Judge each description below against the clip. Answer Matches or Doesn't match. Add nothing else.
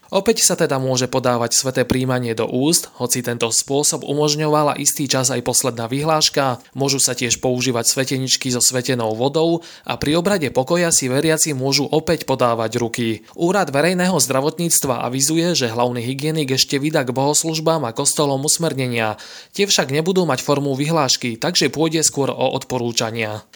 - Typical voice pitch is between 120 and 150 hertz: Matches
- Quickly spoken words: Doesn't match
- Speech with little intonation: Doesn't match